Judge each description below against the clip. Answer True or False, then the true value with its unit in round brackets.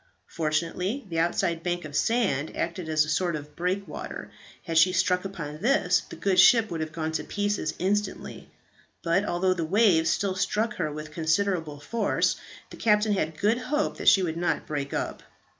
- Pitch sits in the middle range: True (175 Hz)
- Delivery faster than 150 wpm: True (180 wpm)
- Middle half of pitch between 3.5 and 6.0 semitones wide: True (4.1 semitones)